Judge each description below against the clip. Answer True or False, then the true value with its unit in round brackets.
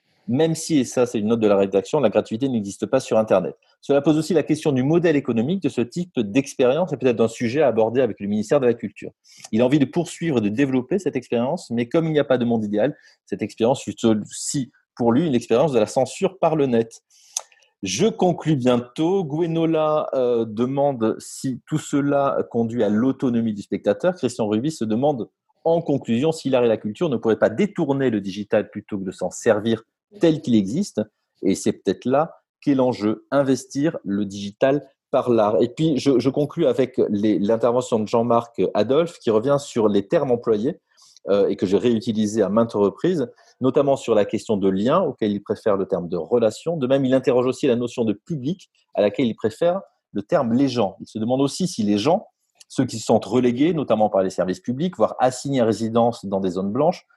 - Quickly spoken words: False (210 wpm)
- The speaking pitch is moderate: False (125 Hz)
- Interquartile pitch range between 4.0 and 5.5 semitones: True (5.0 semitones)